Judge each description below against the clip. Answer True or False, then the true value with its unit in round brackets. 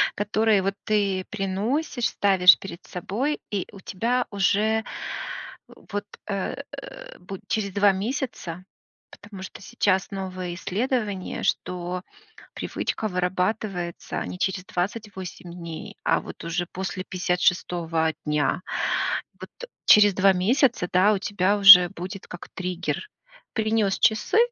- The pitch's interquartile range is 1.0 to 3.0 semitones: True (2.7 semitones)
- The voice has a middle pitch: False (195 Hz)